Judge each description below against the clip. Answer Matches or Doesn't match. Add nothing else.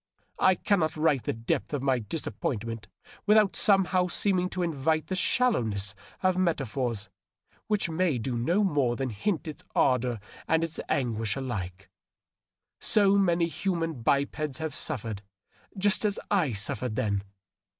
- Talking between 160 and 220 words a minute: Doesn't match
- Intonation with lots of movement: Matches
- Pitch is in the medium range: Matches